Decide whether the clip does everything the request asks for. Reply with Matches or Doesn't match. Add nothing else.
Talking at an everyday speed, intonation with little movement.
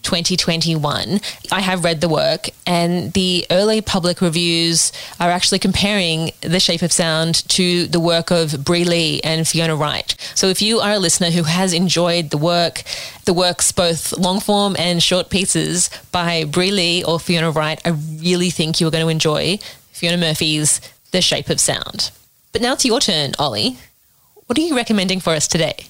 Matches